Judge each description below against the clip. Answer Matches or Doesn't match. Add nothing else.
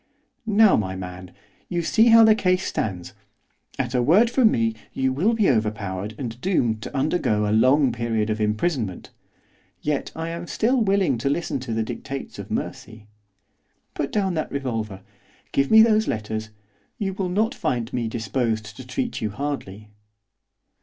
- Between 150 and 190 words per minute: Matches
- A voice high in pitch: Doesn't match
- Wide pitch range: Matches